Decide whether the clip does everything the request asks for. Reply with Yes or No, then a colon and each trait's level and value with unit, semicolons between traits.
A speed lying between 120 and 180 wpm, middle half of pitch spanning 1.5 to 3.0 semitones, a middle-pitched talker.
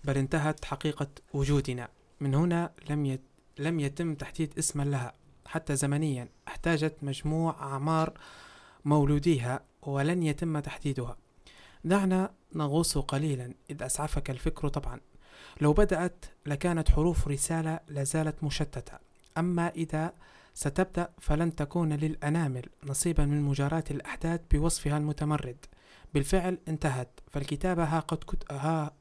No: average, 110 wpm; narrow, 2.6 semitones; medium, 150 Hz